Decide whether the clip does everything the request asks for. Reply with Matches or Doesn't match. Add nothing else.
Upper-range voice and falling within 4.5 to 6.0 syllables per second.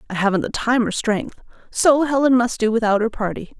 Matches